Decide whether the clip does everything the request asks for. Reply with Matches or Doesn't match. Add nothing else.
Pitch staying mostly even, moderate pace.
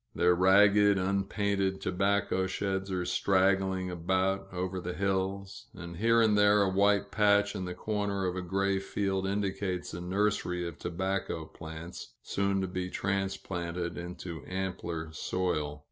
Matches